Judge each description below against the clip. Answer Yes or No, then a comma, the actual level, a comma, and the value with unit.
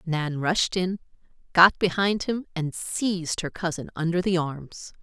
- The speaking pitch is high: No, medium, 175 Hz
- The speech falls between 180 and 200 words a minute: No, average, 155 wpm